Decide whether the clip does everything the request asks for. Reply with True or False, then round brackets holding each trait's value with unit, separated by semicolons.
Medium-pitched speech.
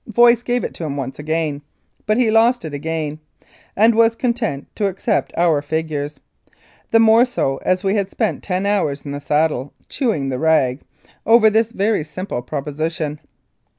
True (180 Hz)